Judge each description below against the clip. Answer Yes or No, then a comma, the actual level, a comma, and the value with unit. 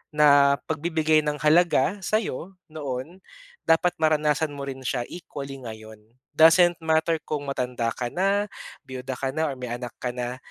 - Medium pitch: Yes, medium, 150 Hz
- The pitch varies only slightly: No, average, 3.9 semitones